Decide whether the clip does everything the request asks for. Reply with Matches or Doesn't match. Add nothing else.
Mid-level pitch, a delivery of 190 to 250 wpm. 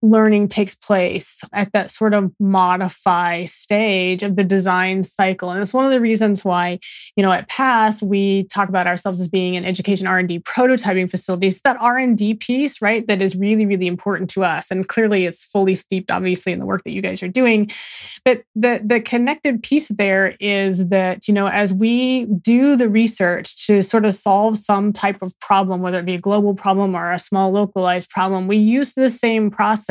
Doesn't match